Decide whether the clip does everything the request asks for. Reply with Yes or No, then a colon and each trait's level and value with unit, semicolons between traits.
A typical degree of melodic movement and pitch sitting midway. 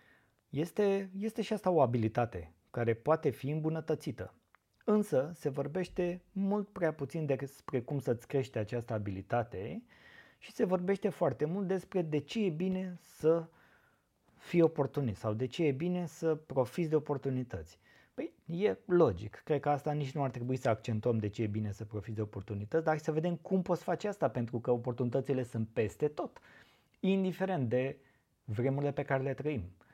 No: wide, 6.2 semitones; medium, 145 Hz